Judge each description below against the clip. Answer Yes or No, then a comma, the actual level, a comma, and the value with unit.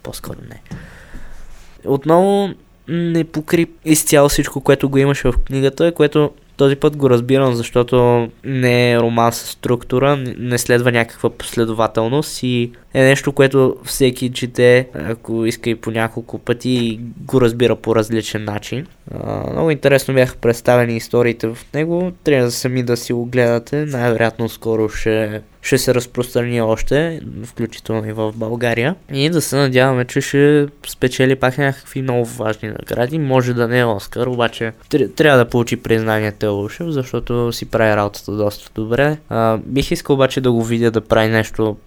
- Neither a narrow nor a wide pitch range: Yes, average, 3.3 semitones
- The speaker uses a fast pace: No, average, 155 wpm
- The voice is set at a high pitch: No, low, 125 Hz